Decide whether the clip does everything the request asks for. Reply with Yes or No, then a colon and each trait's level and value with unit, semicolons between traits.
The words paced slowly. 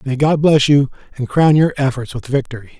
No: fast, 215 wpm